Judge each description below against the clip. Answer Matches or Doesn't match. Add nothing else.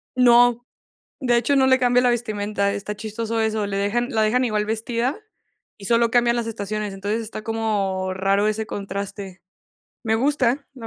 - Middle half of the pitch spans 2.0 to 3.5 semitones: Matches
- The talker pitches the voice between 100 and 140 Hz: Doesn't match